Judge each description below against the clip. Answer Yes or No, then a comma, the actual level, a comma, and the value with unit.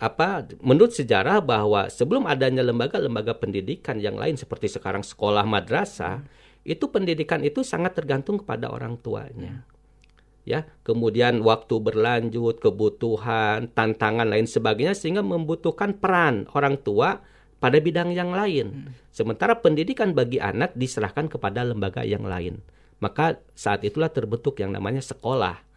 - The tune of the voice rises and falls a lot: Yes, wide, 6.0 semitones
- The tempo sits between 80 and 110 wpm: No, average, 130 wpm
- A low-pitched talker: Yes, low, 125 Hz